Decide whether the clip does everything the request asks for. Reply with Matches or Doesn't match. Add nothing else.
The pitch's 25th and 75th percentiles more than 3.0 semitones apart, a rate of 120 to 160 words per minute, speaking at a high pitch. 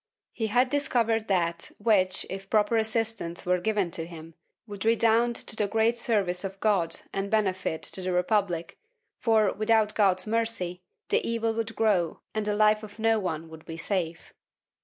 Doesn't match